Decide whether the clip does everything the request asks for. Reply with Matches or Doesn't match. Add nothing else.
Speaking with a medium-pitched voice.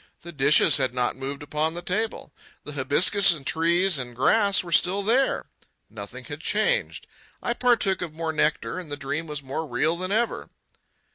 Matches